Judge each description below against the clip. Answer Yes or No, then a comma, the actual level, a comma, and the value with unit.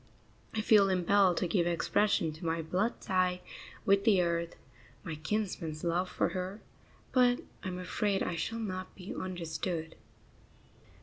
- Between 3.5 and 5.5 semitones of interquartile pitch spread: No, average, 2.9 semitones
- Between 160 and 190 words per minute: No, average, 145 wpm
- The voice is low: No, medium, 185 Hz